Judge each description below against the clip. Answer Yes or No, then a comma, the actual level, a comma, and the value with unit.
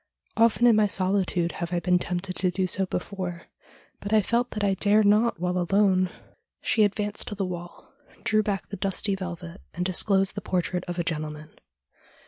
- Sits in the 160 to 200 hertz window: Yes, high, 190 Hz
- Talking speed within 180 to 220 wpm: Yes, average, 185 wpm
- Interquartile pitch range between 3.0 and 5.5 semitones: No, narrow, 2.5 semitones